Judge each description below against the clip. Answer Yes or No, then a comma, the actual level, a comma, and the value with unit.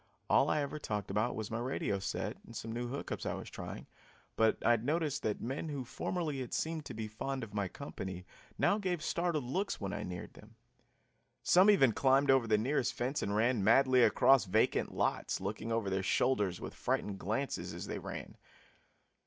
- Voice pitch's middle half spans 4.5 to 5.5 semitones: Yes, average, 4.9 semitones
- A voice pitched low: Yes, low, 120 Hz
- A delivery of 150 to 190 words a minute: No, average, 200 wpm